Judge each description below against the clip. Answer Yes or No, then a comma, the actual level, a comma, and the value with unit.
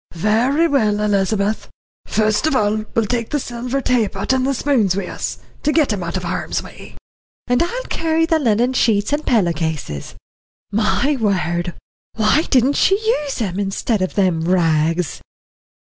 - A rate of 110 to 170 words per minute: Yes, average, 160 wpm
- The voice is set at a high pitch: Yes, high, 215 Hz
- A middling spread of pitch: No, wide, 6.2 semitones